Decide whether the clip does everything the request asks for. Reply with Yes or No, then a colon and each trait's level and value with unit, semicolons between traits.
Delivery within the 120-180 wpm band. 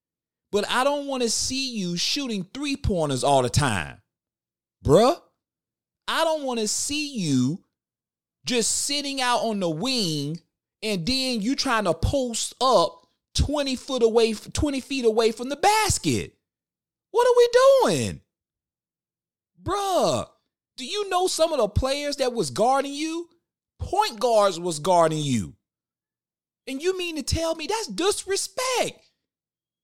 Yes: average, 140 wpm